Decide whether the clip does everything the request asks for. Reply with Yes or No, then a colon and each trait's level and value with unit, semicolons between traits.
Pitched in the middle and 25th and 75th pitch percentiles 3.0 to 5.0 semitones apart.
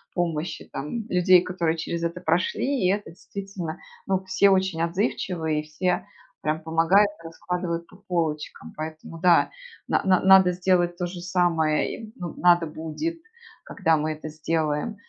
No: medium, 175 Hz; narrow, 2.6 semitones